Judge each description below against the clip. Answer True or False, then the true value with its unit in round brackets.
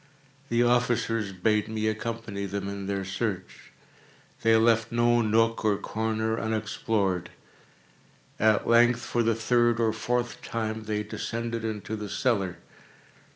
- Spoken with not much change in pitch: True (1.8 semitones)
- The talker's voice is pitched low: True (110 Hz)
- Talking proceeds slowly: True (130 wpm)